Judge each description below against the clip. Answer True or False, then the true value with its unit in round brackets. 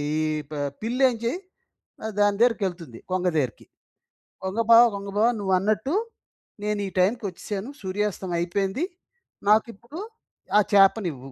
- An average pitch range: True (3.4 semitones)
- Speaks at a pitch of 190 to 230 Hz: True (200 Hz)